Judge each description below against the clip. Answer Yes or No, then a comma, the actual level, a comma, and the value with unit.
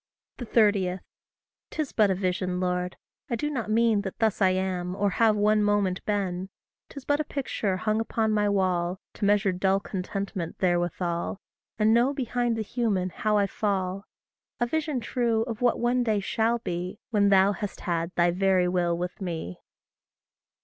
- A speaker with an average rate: Yes, average, 170 wpm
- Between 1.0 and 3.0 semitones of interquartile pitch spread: No, average, 3.5 semitones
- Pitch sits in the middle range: No, high, 200 Hz